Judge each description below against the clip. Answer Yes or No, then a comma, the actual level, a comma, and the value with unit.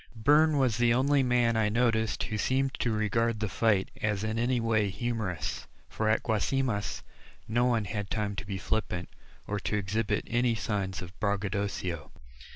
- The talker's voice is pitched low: Yes, low, 110 Hz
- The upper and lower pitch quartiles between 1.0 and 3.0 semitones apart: Yes, average, 2.7 semitones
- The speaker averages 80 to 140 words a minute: No, average, 165 wpm